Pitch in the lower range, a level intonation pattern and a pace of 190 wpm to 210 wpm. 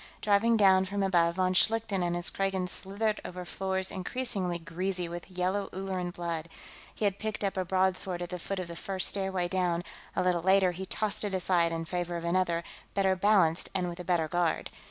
No: medium, 185 Hz; narrow, 1.8 semitones; average, 200 wpm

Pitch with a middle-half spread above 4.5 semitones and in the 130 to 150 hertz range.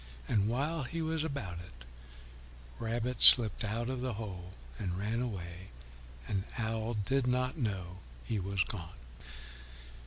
No: average, 4.9 semitones; low, 110 Hz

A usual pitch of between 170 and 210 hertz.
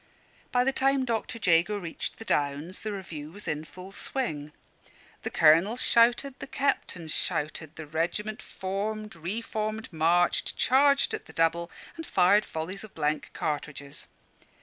Yes: medium, 185 Hz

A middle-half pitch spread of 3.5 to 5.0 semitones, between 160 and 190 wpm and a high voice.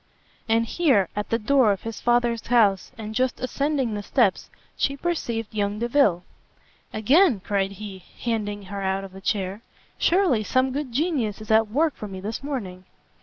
Yes: average, 4.3 semitones; average, 170 wpm; high, 225 Hz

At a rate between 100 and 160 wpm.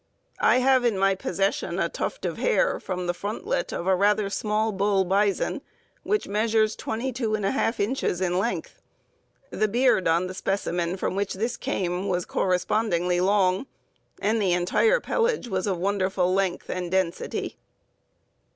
Yes: average, 150 wpm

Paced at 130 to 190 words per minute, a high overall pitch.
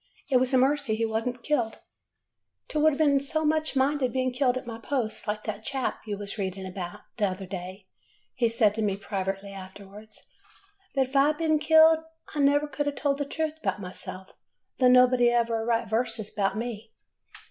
No: fast, 205 wpm; high, 240 Hz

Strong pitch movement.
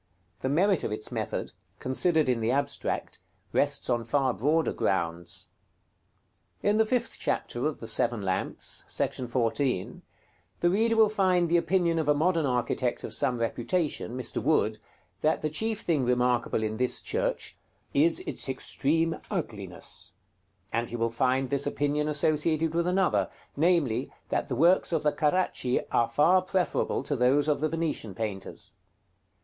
Yes: wide, 5.8 semitones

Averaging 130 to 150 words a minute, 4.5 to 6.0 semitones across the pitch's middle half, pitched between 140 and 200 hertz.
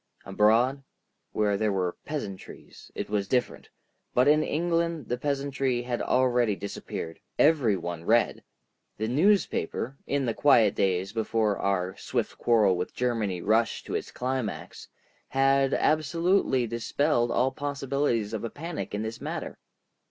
No: slow, 135 wpm; average, 4.9 semitones; low, 120 Hz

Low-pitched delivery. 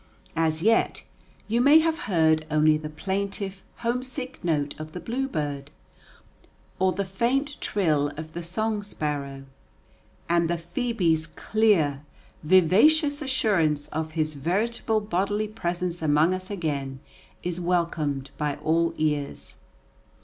No: medium, 175 Hz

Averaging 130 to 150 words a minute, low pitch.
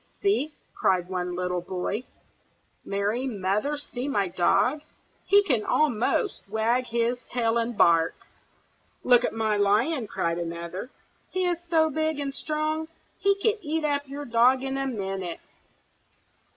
No: average, 140 wpm; high, 240 Hz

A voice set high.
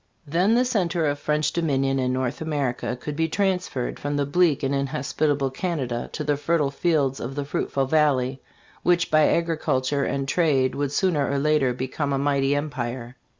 No: medium, 145 Hz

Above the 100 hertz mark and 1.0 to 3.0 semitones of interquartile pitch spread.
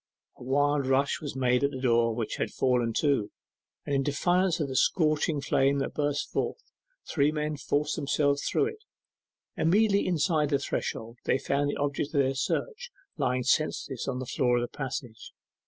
Yes: medium, 140 Hz; average, 2.7 semitones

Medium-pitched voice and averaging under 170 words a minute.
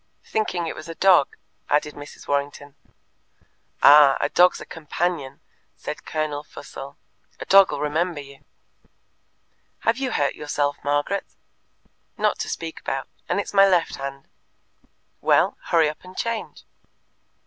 Yes: medium, 150 Hz; slow, 135 wpm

